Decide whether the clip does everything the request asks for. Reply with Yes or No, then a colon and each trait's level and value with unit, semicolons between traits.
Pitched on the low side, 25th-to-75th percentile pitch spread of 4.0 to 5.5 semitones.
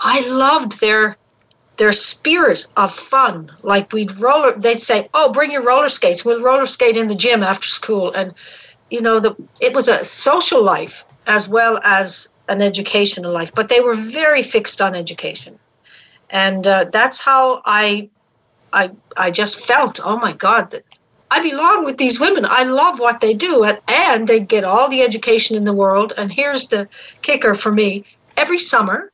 No: high, 225 Hz; average, 4.4 semitones